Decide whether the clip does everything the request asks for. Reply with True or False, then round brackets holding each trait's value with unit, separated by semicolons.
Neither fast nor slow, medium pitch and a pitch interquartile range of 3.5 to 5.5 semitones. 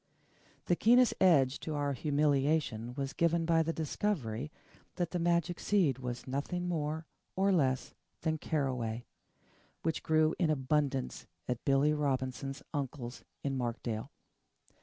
False (130 wpm; 145 Hz; 3.8 semitones)